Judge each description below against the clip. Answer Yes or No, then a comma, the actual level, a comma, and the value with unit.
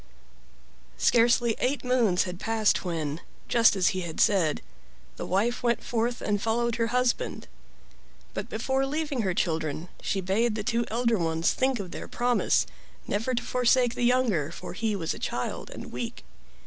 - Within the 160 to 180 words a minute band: Yes, average, 165 wpm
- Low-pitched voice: No, high, 225 Hz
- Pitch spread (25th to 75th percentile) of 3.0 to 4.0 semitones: No, average, 4.8 semitones